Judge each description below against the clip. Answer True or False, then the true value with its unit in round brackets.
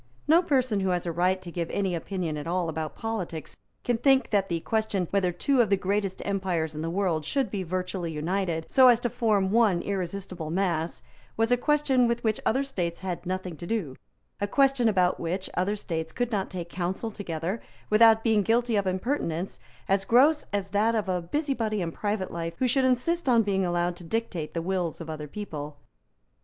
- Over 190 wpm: True (200 wpm)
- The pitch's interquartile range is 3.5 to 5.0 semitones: True (4.7 semitones)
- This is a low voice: False (190 Hz)